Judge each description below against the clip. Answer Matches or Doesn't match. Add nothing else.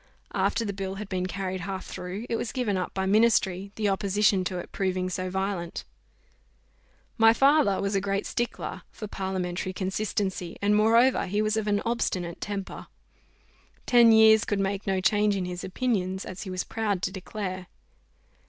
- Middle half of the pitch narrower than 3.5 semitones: Matches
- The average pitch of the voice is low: Doesn't match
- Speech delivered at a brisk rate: Doesn't match